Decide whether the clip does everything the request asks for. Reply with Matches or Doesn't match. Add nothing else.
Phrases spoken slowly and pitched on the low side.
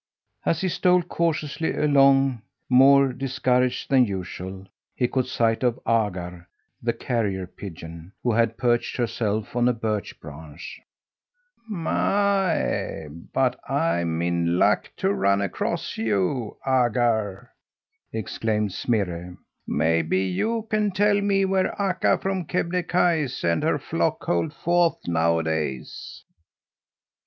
Matches